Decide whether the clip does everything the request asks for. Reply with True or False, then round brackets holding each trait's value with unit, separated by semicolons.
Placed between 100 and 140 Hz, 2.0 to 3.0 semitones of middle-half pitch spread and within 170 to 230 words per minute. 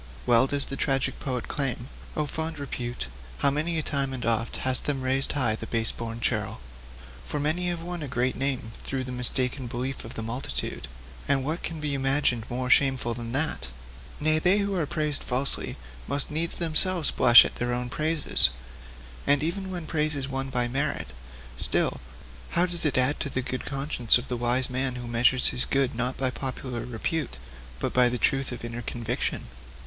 False (135 Hz; 3.5 semitones; 195 wpm)